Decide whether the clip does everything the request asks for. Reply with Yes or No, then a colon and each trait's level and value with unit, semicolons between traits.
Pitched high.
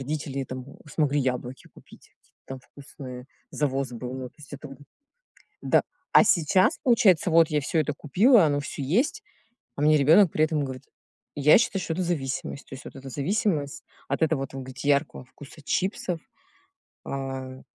No: medium, 145 Hz